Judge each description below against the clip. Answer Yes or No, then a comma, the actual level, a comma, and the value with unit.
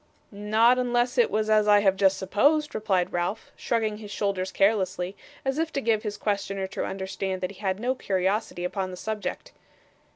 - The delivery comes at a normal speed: Yes, average, 185 wpm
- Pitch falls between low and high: No, high, 205 Hz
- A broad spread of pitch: No, average, 2.7 semitones